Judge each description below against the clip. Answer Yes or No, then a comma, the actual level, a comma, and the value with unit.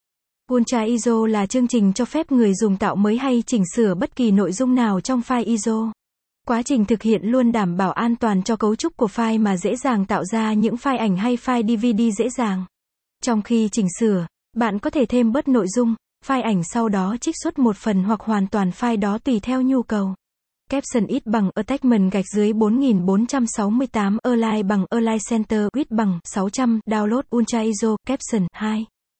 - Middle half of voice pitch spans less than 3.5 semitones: Yes, narrow, 2.6 semitones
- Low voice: No, high, 225 Hz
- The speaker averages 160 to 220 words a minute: Yes, average, 195 wpm